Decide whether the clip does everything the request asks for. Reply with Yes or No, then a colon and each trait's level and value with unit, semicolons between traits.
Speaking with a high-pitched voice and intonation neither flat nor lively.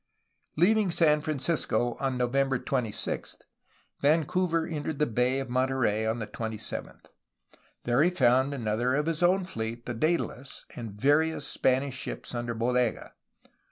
No: low, 130 Hz; average, 4.3 semitones